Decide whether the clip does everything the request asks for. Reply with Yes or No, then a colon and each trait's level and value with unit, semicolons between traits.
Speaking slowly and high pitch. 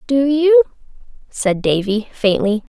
Yes: slow, 105 wpm; very high, 250 Hz